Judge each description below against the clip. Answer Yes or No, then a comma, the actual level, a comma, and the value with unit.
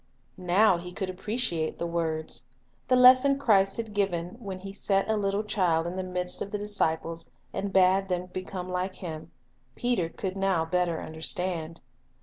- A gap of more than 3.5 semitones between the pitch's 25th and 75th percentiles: No, average, 2.8 semitones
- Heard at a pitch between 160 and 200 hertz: Yes, medium, 185 Hz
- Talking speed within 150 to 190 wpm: Yes, average, 175 wpm